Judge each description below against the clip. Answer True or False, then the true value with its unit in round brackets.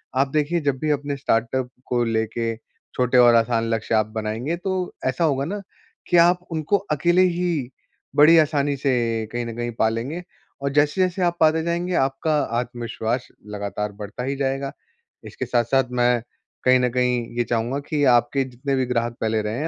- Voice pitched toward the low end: True (130 Hz)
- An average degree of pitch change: True (4.5 semitones)